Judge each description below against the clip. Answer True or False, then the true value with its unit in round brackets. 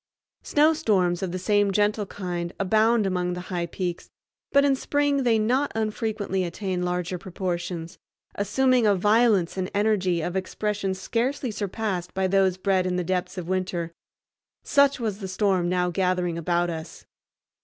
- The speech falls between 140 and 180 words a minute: True (155 wpm)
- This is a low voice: False (190 Hz)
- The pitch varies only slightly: False (3.2 semitones)